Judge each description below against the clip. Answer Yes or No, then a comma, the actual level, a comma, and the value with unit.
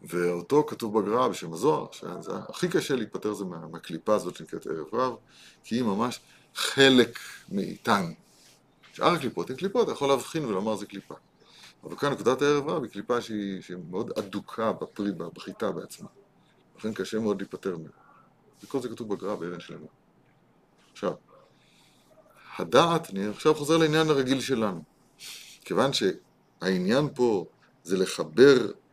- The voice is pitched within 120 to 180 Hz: No, low, 105 Hz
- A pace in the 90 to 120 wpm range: No, average, 145 wpm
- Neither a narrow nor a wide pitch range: No, wide, 6.2 semitones